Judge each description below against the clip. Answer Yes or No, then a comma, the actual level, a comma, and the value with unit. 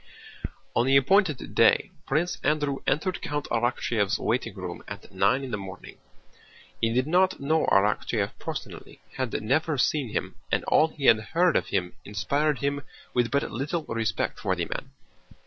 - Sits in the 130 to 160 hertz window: Yes, low, 135 Hz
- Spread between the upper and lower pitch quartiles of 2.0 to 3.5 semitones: No, average, 5.1 semitones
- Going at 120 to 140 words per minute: No, average, 165 wpm